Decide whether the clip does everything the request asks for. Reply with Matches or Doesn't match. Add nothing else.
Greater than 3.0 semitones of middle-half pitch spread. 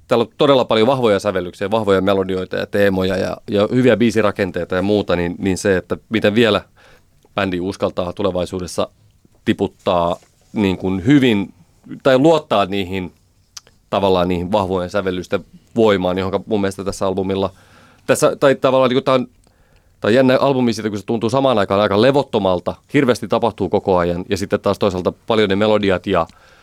Doesn't match